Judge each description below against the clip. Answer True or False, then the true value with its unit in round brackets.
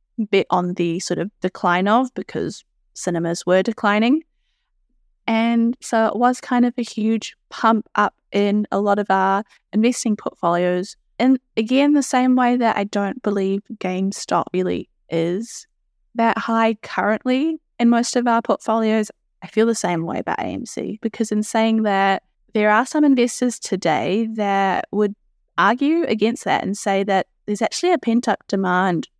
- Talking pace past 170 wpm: False (160 wpm)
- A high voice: True (220 Hz)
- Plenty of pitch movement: False (3.7 semitones)